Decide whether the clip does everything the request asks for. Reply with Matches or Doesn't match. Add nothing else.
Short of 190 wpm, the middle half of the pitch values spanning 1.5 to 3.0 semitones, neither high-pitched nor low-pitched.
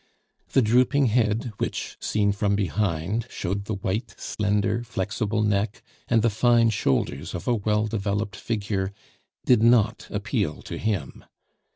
Doesn't match